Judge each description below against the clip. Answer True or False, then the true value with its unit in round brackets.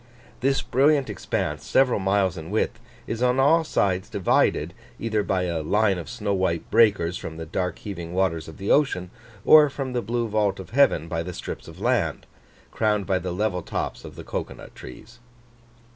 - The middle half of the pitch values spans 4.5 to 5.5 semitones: True (4.8 semitones)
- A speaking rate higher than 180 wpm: True (190 wpm)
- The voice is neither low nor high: False (100 Hz)